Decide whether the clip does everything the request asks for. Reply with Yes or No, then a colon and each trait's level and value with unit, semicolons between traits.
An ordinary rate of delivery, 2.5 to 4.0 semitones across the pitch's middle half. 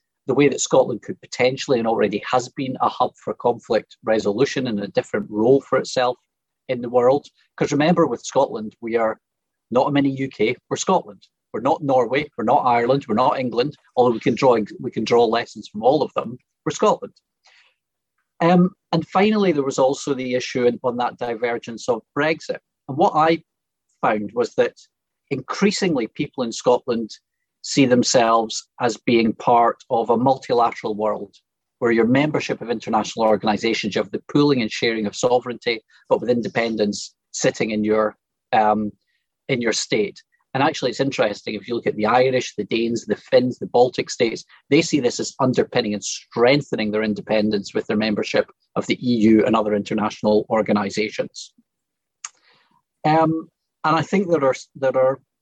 No: average, 170 wpm; average, 4.8 semitones